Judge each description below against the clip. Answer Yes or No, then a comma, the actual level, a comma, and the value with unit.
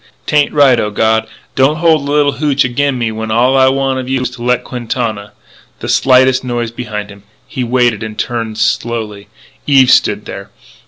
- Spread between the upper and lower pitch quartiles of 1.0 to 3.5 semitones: Yes, average, 3.2 semitones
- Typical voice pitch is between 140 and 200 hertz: No, low, 125 Hz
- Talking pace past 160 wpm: Yes, average, 190 wpm